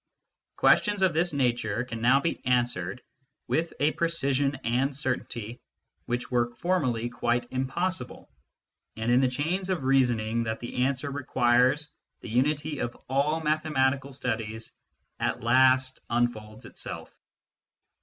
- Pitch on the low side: Yes, low, 130 Hz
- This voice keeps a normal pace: No, slow, 125 wpm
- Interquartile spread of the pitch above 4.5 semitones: No, average, 3.3 semitones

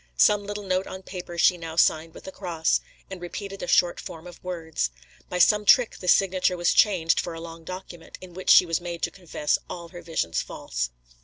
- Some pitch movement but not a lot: No, narrow, 2.2 semitones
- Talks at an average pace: No, fast, 215 wpm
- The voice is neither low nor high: Yes, medium, 175 Hz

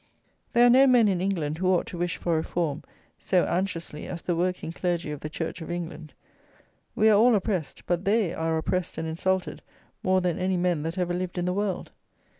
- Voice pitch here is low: No, medium, 180 Hz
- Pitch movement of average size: No, narrow, 2.3 semitones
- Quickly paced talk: Yes, fast, 210 wpm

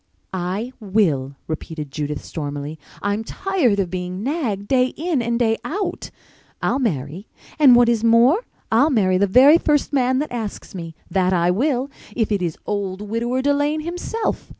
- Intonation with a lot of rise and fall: Yes, wide, 6.4 semitones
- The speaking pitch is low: No, high, 225 Hz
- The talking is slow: No, average, 155 wpm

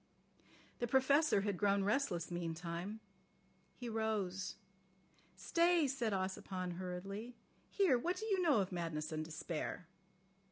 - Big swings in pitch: Yes, wide, 6.5 semitones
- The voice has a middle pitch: No, high, 200 Hz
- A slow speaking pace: Yes, slow, 120 wpm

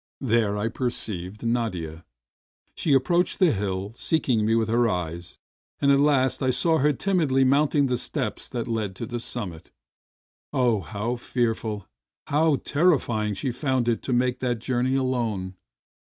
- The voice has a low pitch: Yes, low, 120 Hz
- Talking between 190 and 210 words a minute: No, average, 155 wpm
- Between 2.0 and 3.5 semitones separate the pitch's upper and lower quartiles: No, average, 4.0 semitones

